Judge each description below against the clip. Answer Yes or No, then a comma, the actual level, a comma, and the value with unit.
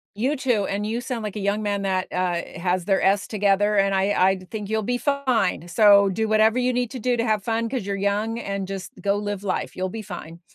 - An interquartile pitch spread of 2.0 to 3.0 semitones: Yes, narrow, 2.5 semitones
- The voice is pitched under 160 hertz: No, high, 205 Hz